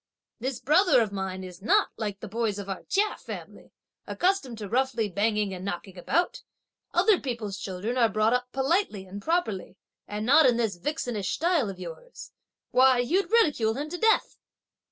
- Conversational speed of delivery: Yes, average, 175 wpm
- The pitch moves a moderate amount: No, wide, 6.7 semitones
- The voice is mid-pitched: No, high, 230 Hz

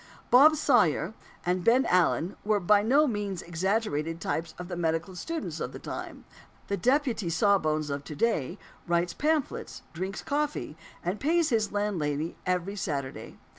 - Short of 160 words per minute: Yes, average, 150 wpm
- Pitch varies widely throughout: Yes, wide, 5.7 semitones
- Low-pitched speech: No, high, 190 Hz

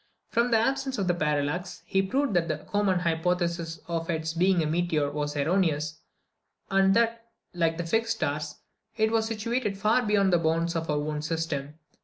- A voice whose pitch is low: No, medium, 175 Hz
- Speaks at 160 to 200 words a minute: Yes, average, 175 wpm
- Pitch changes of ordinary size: Yes, average, 4.7 semitones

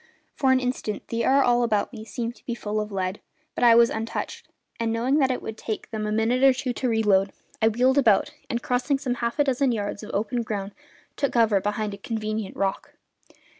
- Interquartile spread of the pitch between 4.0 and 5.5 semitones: No, average, 2.8 semitones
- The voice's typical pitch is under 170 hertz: No, high, 230 Hz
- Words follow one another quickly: Yes, fast, 215 wpm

